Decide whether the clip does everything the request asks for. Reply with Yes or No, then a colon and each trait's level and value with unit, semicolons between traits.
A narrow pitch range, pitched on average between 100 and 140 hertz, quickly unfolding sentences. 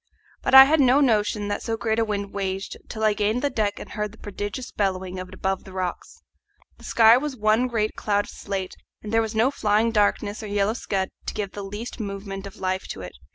No: narrow, 2.3 semitones; high, 210 Hz; fast, 235 wpm